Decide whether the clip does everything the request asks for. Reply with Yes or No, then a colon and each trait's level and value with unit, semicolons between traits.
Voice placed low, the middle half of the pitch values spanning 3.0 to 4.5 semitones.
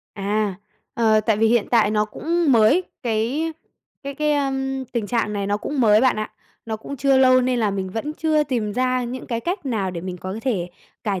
No: high, 235 Hz; average, 4.1 semitones